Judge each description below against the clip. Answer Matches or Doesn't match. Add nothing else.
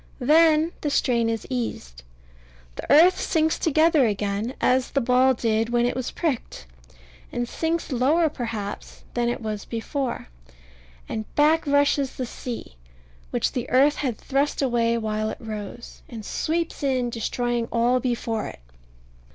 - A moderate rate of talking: Matches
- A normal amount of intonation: Matches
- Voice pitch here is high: Matches